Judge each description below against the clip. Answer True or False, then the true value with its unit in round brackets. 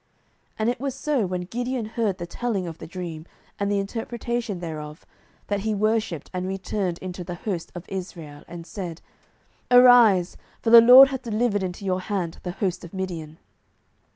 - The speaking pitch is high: True (195 Hz)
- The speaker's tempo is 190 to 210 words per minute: False (180 wpm)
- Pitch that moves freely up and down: False (4.5 semitones)